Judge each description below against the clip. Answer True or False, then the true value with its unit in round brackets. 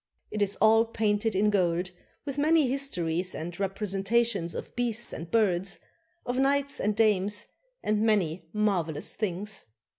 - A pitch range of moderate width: True (3.8 semitones)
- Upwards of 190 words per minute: False (140 wpm)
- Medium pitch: False (210 Hz)